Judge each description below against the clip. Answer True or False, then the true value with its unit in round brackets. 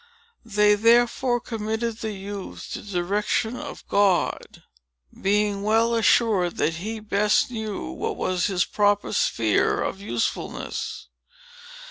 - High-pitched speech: True (210 Hz)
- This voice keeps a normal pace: False (120 wpm)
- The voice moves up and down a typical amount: False (2.2 semitones)